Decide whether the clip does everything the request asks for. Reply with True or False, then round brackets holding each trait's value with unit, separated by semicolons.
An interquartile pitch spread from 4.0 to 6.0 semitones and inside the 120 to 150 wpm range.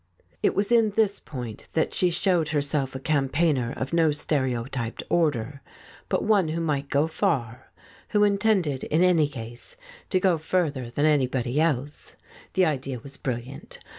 False (4.7 semitones; 160 wpm)